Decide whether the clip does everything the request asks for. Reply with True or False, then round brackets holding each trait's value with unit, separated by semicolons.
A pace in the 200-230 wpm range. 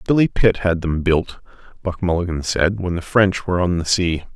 True (205 wpm)